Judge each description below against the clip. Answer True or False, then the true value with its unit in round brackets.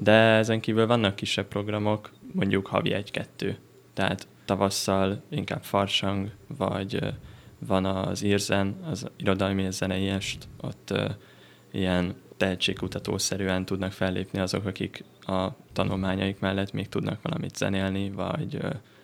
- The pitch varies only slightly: True (1.4 semitones)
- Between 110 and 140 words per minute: True (125 wpm)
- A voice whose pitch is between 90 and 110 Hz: True (95 Hz)